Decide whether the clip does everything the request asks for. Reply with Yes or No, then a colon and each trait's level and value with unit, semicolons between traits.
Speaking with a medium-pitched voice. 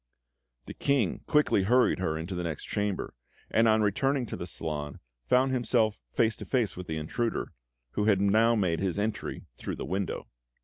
No: low, 105 Hz